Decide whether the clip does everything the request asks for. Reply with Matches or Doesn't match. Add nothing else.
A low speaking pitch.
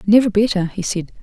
Doesn't match